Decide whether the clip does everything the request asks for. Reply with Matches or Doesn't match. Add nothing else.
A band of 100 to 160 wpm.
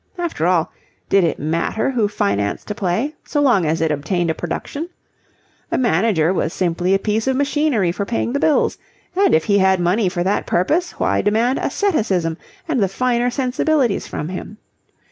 Doesn't match